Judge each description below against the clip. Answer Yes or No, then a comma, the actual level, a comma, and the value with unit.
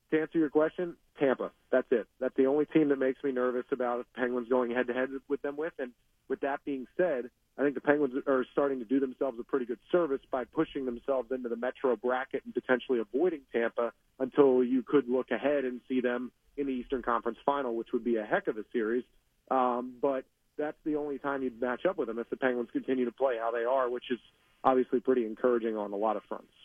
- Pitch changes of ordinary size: No, narrow, 2.3 semitones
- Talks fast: Yes, fast, 235 wpm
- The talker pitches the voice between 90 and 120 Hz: No, low, 130 Hz